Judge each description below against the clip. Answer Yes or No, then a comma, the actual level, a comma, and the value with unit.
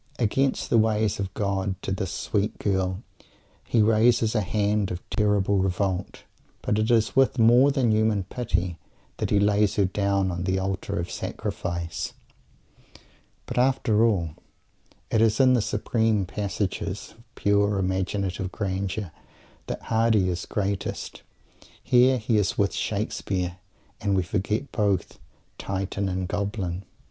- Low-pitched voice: Yes, low, 100 Hz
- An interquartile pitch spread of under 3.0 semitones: Yes, narrow, 2.6 semitones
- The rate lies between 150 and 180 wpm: No, average, 140 wpm